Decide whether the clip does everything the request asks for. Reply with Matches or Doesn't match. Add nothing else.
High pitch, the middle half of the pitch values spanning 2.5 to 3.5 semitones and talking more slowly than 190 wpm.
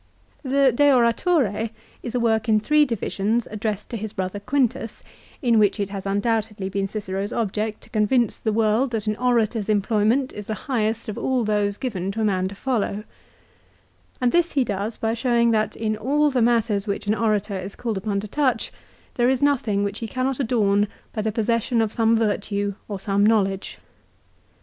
Doesn't match